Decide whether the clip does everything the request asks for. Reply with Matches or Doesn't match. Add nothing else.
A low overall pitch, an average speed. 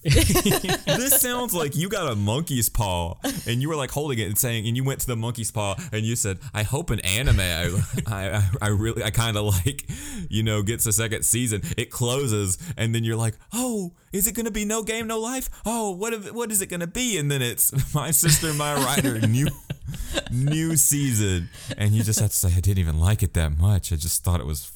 Doesn't match